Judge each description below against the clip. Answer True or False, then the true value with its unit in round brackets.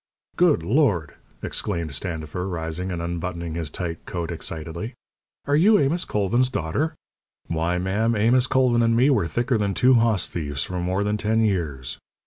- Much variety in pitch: True (5.9 semitones)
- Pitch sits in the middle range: False (95 Hz)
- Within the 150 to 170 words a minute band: True (160 wpm)